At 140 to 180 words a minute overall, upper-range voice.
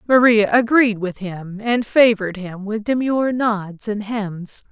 Yes: average, 155 wpm; high, 215 Hz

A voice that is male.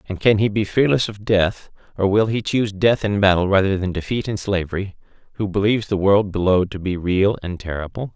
Yes: male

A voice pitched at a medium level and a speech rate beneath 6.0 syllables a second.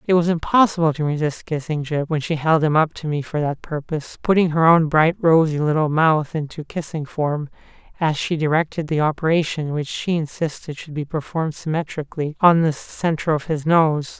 Yes: medium, 155 Hz; 5.3 syllables/s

